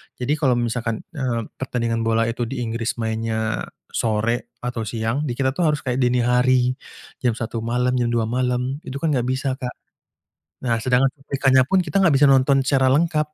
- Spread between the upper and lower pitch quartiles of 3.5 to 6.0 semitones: No, narrow, 2.5 semitones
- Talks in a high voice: No, low, 125 Hz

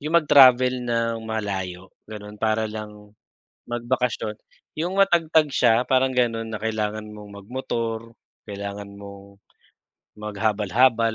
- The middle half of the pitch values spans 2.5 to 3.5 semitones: Yes, average, 3.2 semitones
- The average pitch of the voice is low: Yes, low, 110 Hz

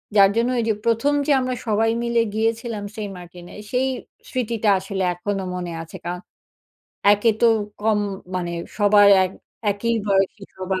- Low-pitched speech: No, high, 205 Hz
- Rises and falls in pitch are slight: No, average, 3.2 semitones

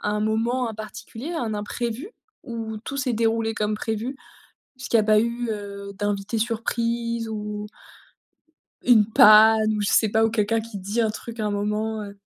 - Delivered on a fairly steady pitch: Yes, narrow, 1.7 semitones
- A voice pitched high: Yes, high, 220 Hz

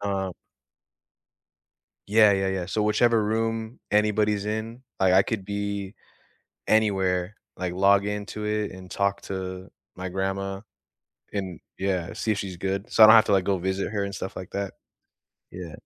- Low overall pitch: Yes, low, 100 Hz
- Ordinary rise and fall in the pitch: No, narrow, 2.0 semitones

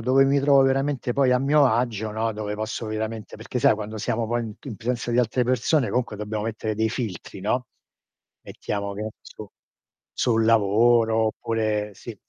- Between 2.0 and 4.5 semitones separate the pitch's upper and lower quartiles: Yes, narrow, 2.6 semitones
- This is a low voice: Yes, low, 115 Hz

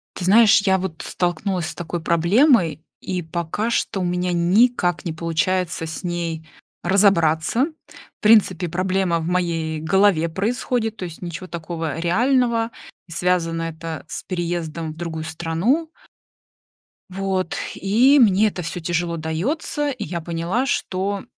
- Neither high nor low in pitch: Yes, medium, 175 Hz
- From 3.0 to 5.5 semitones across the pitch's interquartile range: Yes, average, 3.3 semitones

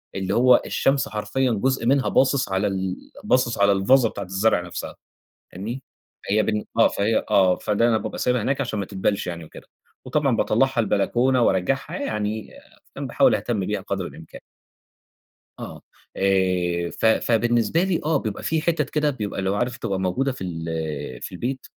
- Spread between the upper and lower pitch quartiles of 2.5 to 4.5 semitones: No, average, 5.2 semitones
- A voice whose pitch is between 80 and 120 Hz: Yes, low, 110 Hz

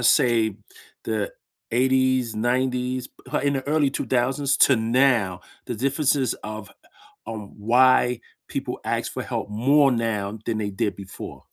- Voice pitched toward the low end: Yes, low, 125 Hz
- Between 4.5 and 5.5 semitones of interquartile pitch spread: No, average, 3.2 semitones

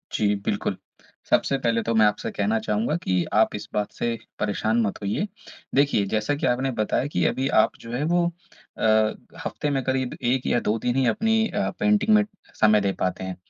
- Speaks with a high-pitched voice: No, low, 115 Hz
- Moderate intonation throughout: Yes, average, 4.6 semitones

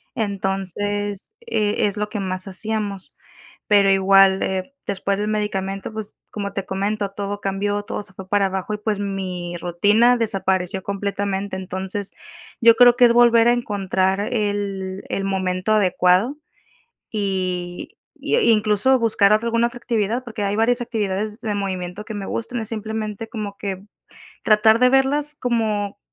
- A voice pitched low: No, high, 205 Hz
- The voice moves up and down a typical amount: No, narrow, 2.3 semitones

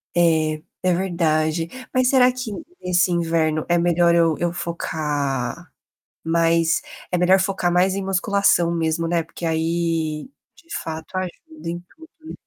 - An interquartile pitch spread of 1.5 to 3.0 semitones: Yes, narrow, 2.4 semitones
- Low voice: No, medium, 170 Hz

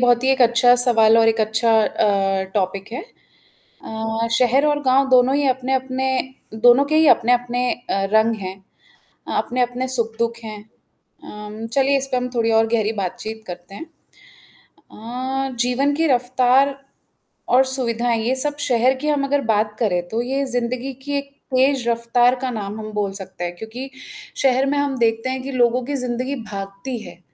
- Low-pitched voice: No, high, 245 Hz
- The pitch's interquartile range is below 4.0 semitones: Yes, average, 2.9 semitones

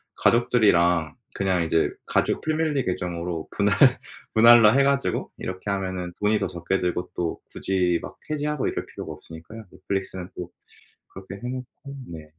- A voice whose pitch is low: Yes, very low, 95 Hz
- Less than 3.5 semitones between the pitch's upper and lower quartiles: No, average, 4.8 semitones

